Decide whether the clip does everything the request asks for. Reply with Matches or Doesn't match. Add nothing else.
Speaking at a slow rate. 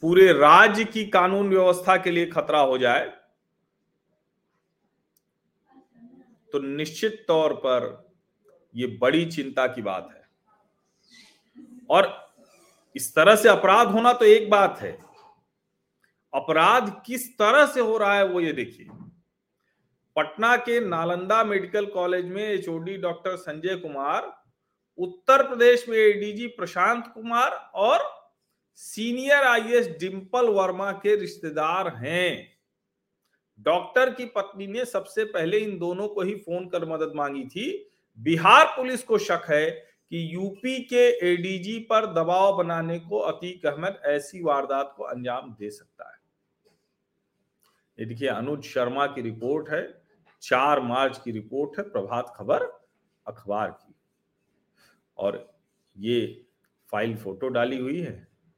Doesn't match